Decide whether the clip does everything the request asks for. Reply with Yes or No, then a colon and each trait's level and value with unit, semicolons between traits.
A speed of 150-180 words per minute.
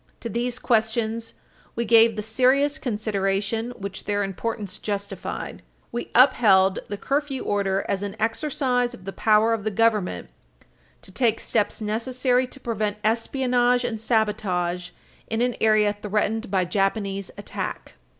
No: average, 140 wpm